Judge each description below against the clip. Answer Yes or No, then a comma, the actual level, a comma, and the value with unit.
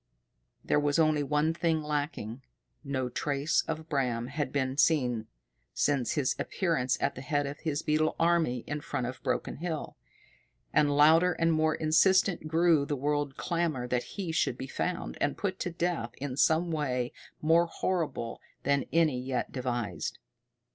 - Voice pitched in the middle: Yes, medium, 150 Hz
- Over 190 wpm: No, average, 160 wpm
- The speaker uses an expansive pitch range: No, average, 3.7 semitones